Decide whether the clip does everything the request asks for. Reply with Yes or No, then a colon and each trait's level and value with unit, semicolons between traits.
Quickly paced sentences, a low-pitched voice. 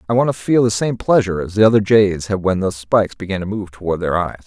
Yes: fast, 280 wpm; low, 100 Hz